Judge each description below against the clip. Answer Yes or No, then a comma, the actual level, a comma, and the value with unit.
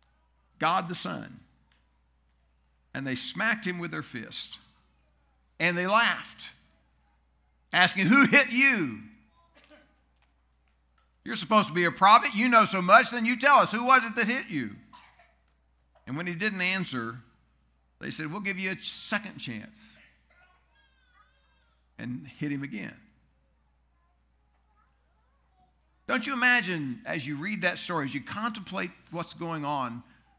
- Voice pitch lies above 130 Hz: Yes, medium, 140 Hz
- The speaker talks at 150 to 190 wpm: No, slow, 135 wpm